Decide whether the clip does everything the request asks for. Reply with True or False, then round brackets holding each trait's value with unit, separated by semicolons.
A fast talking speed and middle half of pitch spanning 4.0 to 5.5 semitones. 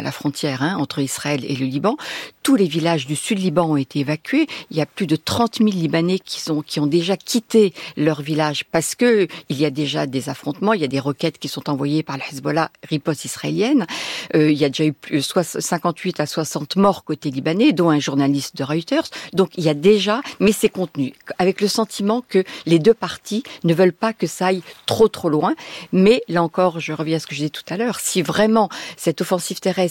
True (235 wpm; 4.5 semitones)